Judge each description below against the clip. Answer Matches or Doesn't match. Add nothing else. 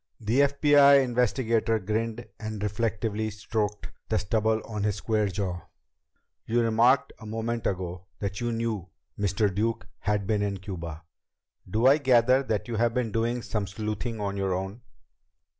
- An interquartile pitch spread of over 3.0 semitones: Doesn't match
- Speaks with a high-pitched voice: Doesn't match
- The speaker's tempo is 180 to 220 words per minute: Doesn't match